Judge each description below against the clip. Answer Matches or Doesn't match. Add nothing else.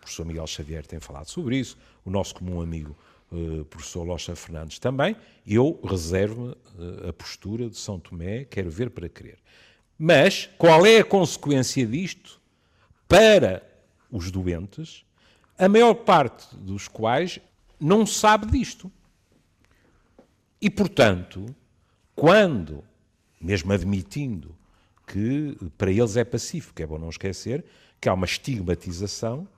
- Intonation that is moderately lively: Doesn't match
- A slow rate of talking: Doesn't match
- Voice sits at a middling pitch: Doesn't match